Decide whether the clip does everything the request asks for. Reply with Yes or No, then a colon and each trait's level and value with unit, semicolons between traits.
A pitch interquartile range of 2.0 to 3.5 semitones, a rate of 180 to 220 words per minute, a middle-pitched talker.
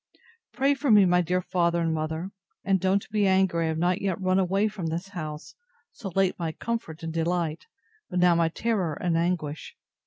Yes: average, 2.9 semitones; average, 195 wpm; medium, 180 Hz